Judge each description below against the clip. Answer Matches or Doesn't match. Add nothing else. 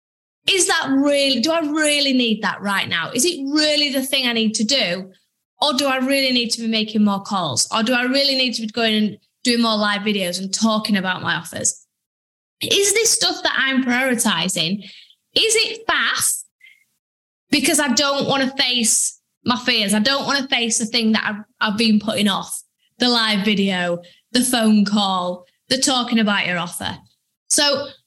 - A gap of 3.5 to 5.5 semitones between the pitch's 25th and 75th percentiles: Matches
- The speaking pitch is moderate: Doesn't match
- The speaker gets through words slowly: Doesn't match